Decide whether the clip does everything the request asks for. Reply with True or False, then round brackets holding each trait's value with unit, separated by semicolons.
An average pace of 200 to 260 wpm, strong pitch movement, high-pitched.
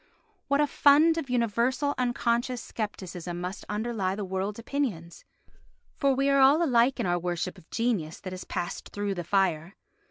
False (165 wpm; 6.1 semitones; 220 Hz)